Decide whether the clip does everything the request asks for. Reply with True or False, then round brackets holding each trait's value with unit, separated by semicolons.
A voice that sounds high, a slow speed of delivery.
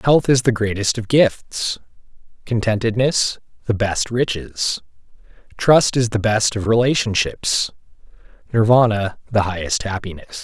False (110 Hz; 115 wpm)